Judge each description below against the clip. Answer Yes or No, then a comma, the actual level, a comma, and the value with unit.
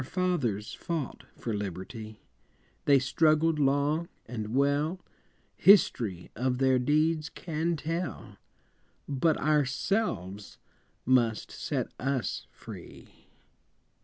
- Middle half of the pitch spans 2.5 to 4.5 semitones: No, average, 5.2 semitones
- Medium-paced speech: No, slow, 95 wpm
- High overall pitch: No, medium, 140 Hz